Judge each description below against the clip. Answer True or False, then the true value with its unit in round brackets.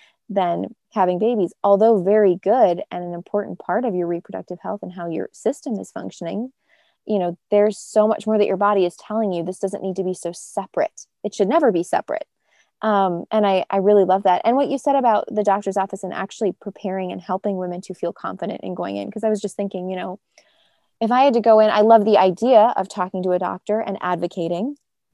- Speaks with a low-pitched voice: False (195 Hz)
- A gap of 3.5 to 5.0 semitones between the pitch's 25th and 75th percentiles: False (2.9 semitones)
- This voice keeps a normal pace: False (225 wpm)